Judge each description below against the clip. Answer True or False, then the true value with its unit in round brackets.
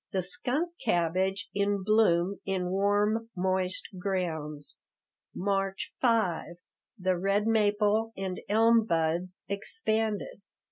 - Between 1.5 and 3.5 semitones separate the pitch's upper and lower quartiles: True (2.9 semitones)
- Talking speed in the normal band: False (100 wpm)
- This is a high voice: True (195 Hz)